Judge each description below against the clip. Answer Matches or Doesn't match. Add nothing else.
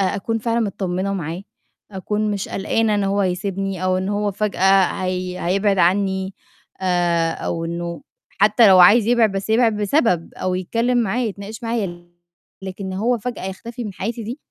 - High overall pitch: Matches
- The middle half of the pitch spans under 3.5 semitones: Matches